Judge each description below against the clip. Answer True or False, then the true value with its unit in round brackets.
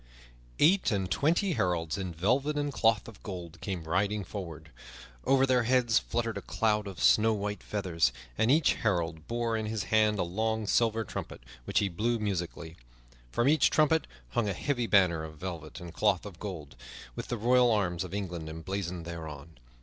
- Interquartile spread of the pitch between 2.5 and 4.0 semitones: False (5.1 semitones)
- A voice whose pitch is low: True (100 Hz)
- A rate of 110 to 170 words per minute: False (180 wpm)